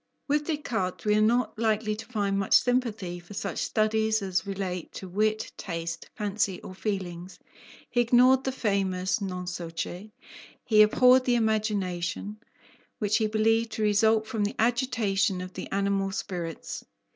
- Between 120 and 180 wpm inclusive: Yes, average, 155 wpm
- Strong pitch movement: No, average, 2.9 semitones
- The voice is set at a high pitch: Yes, high, 210 Hz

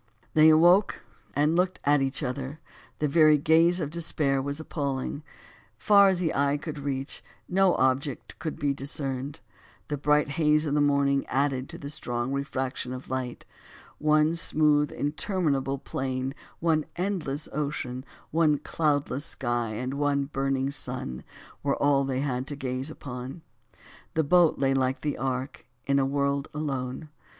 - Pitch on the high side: No, medium, 140 Hz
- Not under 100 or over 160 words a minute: Yes, average, 150 wpm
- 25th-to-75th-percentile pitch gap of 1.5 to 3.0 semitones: Yes, narrow, 2.4 semitones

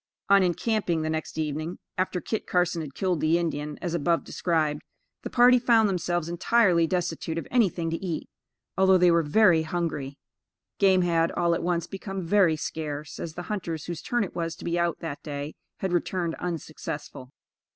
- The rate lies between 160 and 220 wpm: Yes, average, 180 wpm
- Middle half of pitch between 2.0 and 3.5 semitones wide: Yes, narrow, 2.6 semitones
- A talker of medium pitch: Yes, medium, 170 Hz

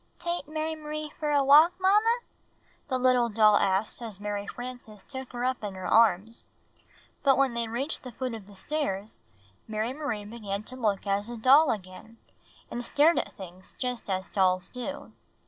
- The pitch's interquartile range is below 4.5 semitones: No, wide, 5.4 semitones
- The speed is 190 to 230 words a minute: No, average, 180 wpm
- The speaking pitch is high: Yes, high, 235 Hz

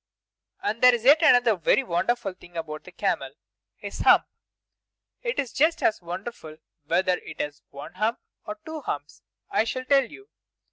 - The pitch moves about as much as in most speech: No, wide, 7.4 semitones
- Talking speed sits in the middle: Yes, average, 170 wpm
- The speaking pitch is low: No, high, 220 Hz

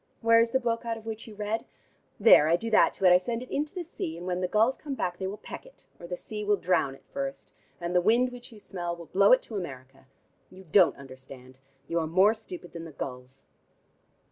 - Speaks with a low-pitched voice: No, high, 190 Hz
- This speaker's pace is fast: Yes, fast, 245 wpm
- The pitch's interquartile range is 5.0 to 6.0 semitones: Yes, average, 5.3 semitones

